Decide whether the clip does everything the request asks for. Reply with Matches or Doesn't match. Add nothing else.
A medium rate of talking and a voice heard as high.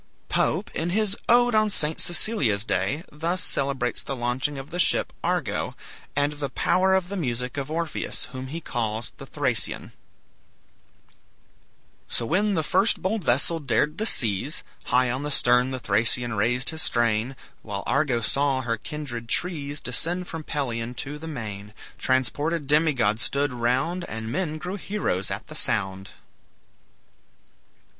Doesn't match